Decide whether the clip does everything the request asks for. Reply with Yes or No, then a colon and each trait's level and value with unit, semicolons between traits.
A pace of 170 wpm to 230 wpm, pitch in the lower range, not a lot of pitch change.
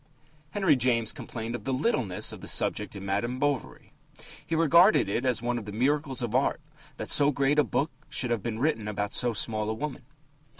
No: fast, 205 wpm; low, 125 Hz; average, 4.6 semitones